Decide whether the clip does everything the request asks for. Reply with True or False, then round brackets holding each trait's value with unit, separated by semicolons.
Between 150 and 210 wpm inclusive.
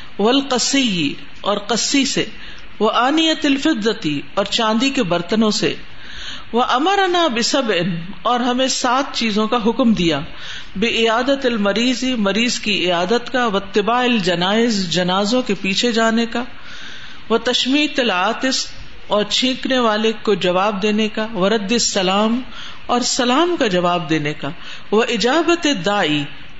False (125 wpm)